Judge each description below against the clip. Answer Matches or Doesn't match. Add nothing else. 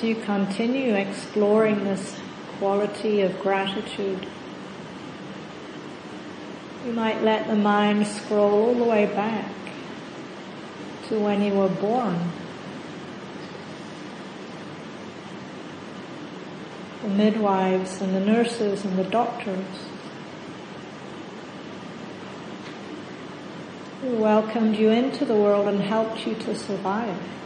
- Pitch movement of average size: Doesn't match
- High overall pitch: Matches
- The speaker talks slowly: Matches